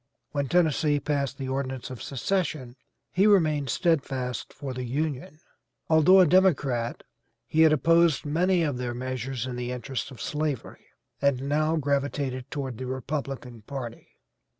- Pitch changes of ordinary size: Yes, average, 3.3 semitones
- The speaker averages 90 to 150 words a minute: Yes, average, 145 wpm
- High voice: No, medium, 140 Hz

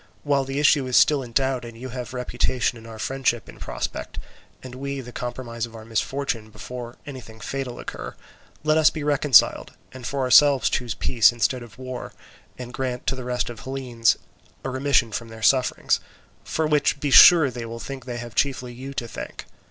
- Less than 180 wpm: No, average, 200 wpm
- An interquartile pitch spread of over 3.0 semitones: No, narrow, 2.4 semitones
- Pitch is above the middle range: No, low, 125 Hz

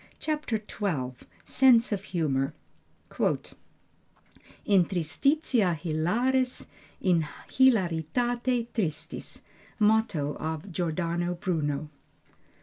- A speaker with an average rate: No, slow, 70 wpm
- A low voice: No, medium, 180 Hz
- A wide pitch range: Yes, wide, 6.7 semitones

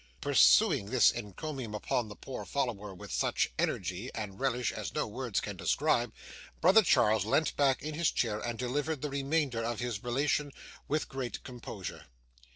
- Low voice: Yes, low, 125 Hz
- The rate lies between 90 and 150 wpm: No, average, 165 wpm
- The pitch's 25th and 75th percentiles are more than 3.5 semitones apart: Yes, average, 4.7 semitones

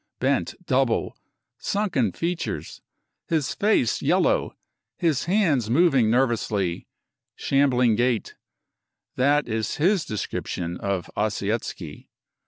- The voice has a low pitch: Yes, low, 125 Hz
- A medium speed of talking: No, slow, 90 wpm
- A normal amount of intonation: No, wide, 6.8 semitones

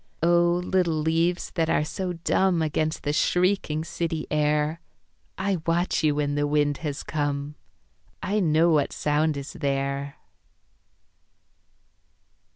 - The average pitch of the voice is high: No, medium, 155 Hz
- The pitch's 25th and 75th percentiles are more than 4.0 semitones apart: No, average, 2.7 semitones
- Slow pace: Yes, slow, 125 wpm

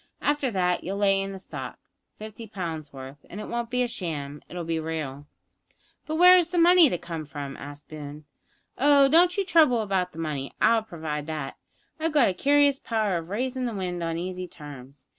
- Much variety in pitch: Yes, wide, 8.2 semitones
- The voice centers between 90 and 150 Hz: No, medium, 185 Hz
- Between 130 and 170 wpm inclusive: No, average, 200 wpm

